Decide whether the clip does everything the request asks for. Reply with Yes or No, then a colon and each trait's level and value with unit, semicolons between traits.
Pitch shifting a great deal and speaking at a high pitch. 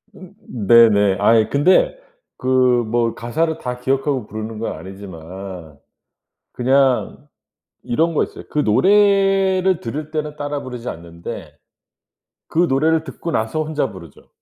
No: wide, 6.5 semitones; low, 130 Hz